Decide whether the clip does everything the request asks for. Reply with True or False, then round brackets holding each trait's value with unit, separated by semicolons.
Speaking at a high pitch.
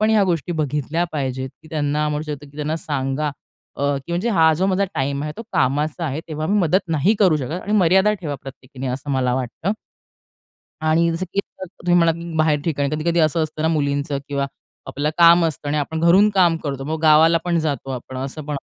False (155 Hz)